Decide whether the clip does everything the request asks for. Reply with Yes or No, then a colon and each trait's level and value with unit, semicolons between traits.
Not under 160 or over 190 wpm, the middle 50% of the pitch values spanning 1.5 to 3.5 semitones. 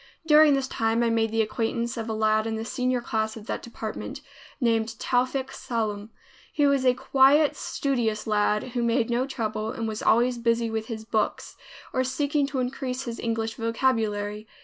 Yes: average, 180 wpm; average, 2.7 semitones